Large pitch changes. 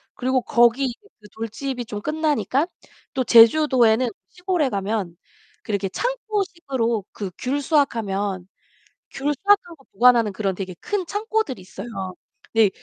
Yes: wide, 6.0 semitones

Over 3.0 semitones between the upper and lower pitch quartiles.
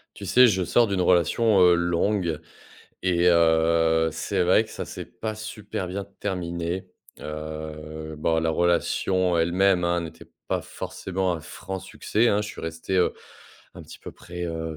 No: average, 2.7 semitones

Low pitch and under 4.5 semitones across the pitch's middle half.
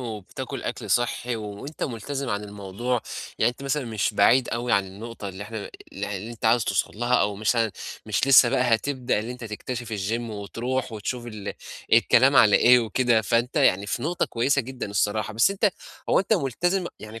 Yes: low, 115 Hz; average, 3.3 semitones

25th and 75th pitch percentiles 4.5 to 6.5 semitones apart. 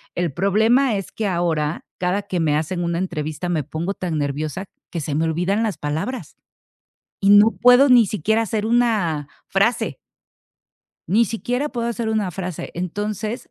Yes: average, 5.2 semitones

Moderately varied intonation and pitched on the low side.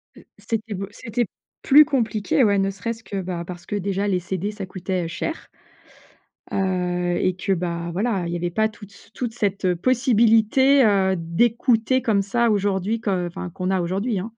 No: average, 3.6 semitones; high, 200 Hz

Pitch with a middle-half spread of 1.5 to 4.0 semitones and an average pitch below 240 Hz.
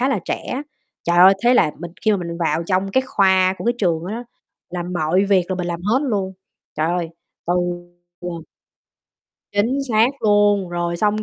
Yes: average, 3.4 semitones; high, 190 Hz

